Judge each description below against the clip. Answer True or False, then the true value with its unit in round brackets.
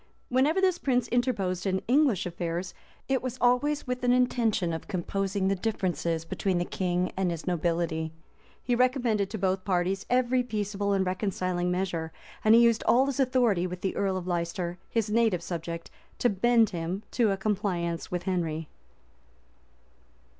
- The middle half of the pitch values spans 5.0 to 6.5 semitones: True (5.3 semitones)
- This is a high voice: True (195 Hz)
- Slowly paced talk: False (160 wpm)